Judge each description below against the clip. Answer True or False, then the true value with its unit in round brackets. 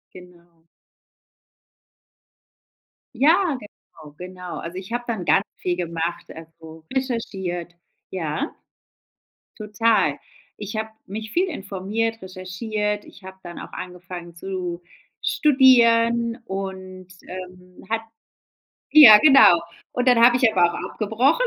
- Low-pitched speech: False (195 Hz)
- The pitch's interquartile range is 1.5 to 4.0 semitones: False (4.5 semitones)